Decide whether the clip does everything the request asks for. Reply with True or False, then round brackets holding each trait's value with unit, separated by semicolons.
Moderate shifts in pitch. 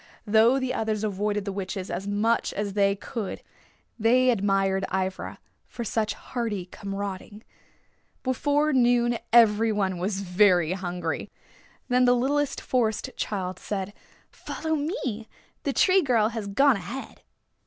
True (3.9 semitones)